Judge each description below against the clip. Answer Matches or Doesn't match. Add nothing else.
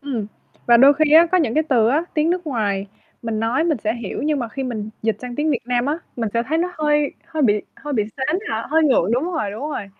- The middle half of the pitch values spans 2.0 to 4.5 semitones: Doesn't match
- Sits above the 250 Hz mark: Matches